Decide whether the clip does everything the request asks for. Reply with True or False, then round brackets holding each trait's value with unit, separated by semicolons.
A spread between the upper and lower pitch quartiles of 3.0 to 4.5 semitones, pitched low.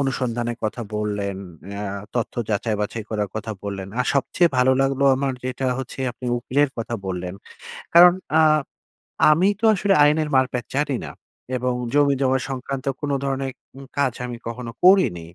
True (3.9 semitones; 130 Hz)